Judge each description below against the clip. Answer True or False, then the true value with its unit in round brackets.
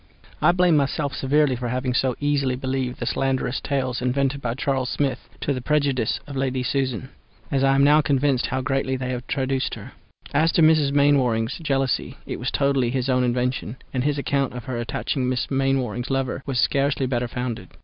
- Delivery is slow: False (190 wpm)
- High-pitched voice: False (135 Hz)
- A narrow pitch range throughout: True (1.8 semitones)